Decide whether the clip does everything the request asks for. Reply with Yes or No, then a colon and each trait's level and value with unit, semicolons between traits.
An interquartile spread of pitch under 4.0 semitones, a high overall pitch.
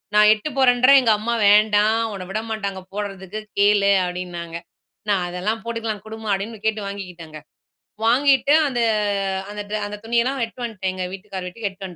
Yes: average, 2.9 semitones; high, 210 Hz